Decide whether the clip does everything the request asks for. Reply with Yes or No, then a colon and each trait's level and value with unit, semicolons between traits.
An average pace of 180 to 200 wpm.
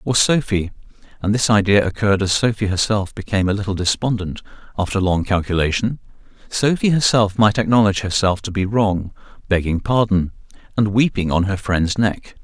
No: average, 145 wpm